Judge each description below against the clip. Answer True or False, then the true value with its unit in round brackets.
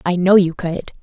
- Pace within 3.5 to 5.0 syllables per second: True (4.8 syllables/s)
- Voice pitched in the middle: True (180 Hz)